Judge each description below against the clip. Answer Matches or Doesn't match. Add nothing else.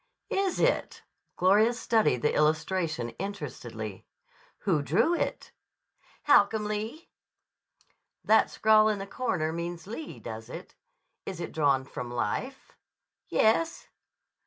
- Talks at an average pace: Doesn't match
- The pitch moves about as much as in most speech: Doesn't match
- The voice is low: Doesn't match